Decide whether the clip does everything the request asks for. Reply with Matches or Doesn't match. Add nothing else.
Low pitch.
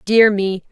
Doesn't match